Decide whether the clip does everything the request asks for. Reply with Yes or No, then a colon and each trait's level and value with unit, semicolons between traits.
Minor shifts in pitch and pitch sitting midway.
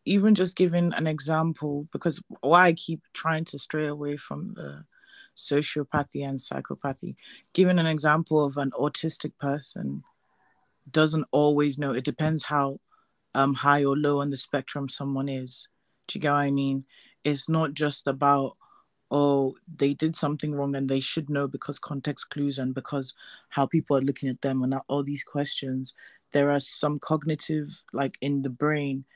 Yes: narrow, 2.2 semitones; medium, 145 Hz